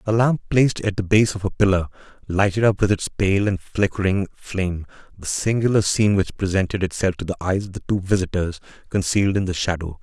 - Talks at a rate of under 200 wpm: No, fast, 205 wpm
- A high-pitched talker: No, very low, 95 Hz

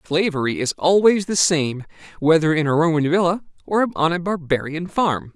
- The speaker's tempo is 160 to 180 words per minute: Yes, average, 170 wpm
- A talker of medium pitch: Yes, medium, 165 Hz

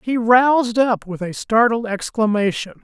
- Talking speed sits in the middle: Yes, average, 150 wpm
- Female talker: No, male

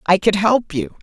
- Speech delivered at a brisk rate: Yes, fast, 235 wpm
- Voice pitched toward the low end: No, high, 205 Hz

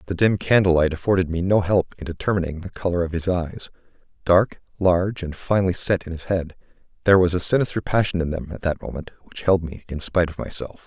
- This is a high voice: No, very low, 90 Hz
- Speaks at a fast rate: Yes, fast, 215 wpm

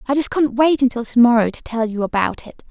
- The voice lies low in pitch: No, high, 245 Hz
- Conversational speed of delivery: No, fast, 265 wpm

